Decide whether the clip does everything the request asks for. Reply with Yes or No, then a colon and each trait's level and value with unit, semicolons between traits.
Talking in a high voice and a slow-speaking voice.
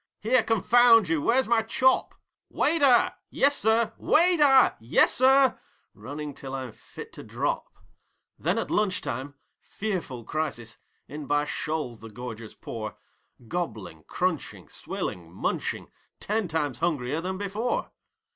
No: medium, 165 Hz; slow, 120 wpm